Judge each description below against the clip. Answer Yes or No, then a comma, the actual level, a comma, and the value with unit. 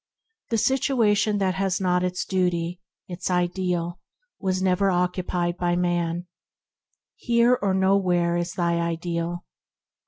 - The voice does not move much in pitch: Yes, narrow, 1.7 semitones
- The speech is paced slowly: Yes, slow, 125 wpm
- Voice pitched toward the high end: No, medium, 180 Hz